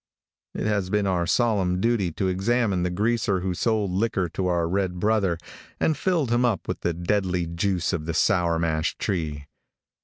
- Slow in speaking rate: No, average, 180 wpm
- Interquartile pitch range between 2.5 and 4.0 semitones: Yes, average, 3.6 semitones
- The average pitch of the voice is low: Yes, very low, 95 Hz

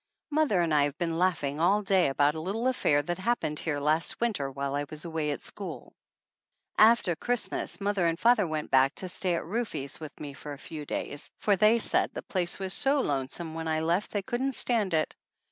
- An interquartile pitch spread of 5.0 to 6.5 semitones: Yes, wide, 5.6 semitones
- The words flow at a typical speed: No, fast, 210 wpm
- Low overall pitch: No, medium, 170 Hz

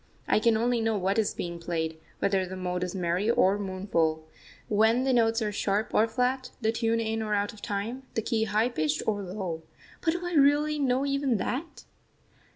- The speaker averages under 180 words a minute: No, average, 200 wpm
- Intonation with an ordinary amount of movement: Yes, average, 4.4 semitones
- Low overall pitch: No, high, 220 Hz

